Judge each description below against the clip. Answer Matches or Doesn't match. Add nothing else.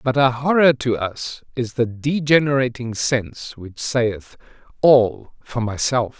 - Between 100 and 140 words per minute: Matches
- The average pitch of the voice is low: Matches